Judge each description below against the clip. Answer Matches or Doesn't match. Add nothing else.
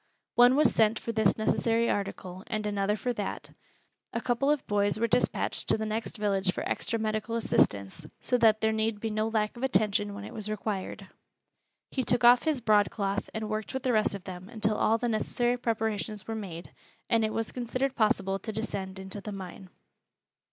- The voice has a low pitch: Doesn't match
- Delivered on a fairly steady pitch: Matches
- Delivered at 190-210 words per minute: Matches